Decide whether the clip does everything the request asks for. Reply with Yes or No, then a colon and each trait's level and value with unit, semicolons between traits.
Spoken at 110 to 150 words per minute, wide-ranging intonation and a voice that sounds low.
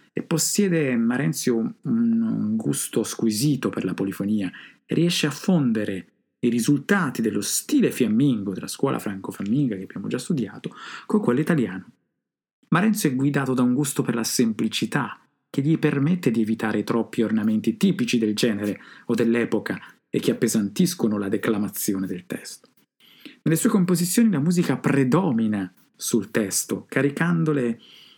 Yes: average, 140 wpm; wide, 6.6 semitones; low, 130 Hz